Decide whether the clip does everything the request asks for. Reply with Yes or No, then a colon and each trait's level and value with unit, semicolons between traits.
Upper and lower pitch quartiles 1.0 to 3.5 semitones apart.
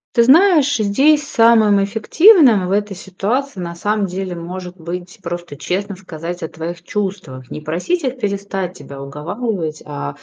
No: average, 4.8 semitones